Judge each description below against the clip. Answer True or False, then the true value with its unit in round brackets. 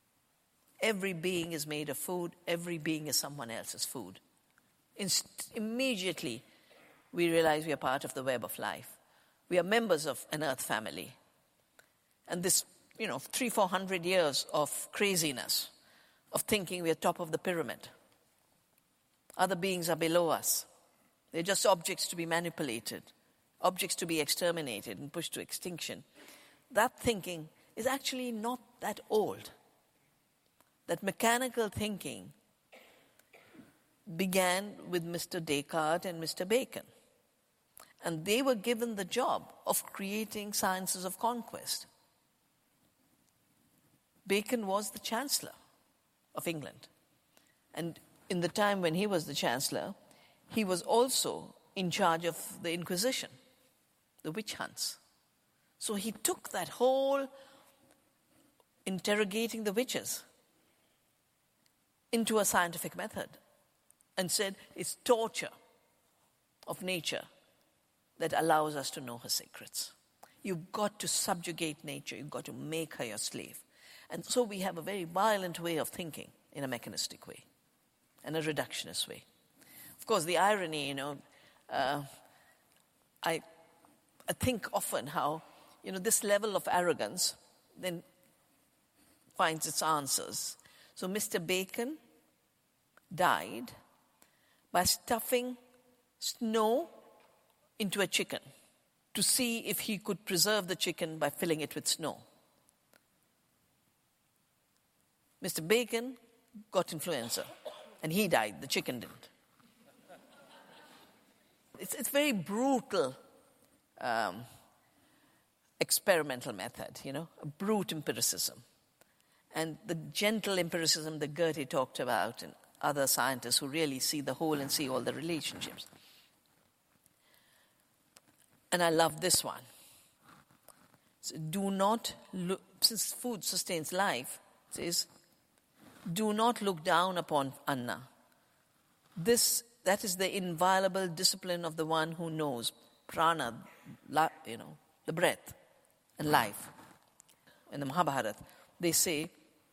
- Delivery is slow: True (125 wpm)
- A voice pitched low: False (185 Hz)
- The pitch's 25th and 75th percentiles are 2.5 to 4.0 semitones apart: False (5.0 semitones)